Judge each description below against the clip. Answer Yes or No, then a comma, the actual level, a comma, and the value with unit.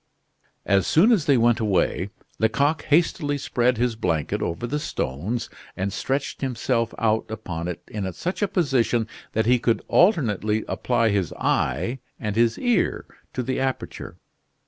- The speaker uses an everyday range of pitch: Yes, average, 4.6 semitones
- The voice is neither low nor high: No, low, 115 Hz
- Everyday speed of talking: Yes, average, 150 wpm